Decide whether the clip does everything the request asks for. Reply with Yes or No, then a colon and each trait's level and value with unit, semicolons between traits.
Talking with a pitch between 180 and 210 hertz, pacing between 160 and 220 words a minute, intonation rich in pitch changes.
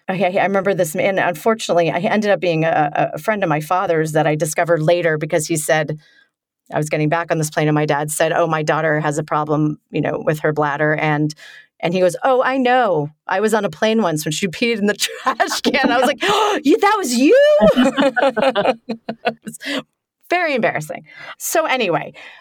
Yes: medium, 185 Hz; fast, 205 wpm; wide, 7.6 semitones